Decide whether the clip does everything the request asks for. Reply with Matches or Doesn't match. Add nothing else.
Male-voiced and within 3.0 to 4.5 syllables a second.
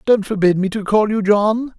Doesn't match